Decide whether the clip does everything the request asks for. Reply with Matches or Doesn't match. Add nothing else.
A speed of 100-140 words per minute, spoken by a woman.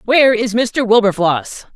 Matches